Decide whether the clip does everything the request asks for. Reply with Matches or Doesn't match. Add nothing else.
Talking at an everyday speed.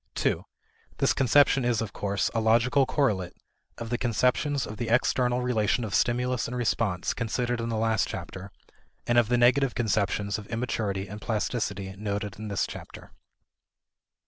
Matches